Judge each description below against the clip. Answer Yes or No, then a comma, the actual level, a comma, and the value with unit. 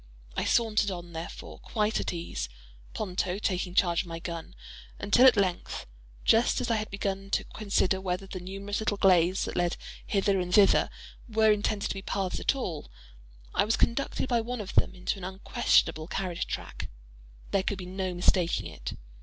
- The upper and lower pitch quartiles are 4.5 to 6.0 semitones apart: No, average, 2.8 semitones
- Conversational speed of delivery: Yes, average, 175 wpm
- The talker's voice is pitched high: Yes, high, 195 Hz